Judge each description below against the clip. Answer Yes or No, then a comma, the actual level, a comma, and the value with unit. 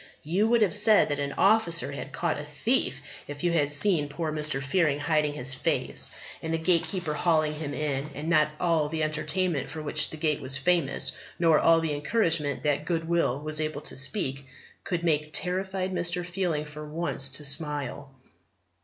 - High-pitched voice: No, medium, 155 Hz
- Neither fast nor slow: Yes, average, 180 wpm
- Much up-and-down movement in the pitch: No, average, 2.8 semitones